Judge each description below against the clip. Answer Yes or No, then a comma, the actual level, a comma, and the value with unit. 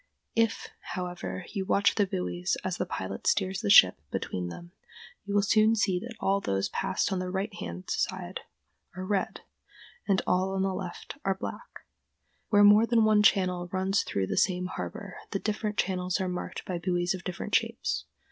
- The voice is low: No, high, 190 Hz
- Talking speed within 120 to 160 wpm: No, average, 185 wpm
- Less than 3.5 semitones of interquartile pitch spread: Yes, narrow, 2.4 semitones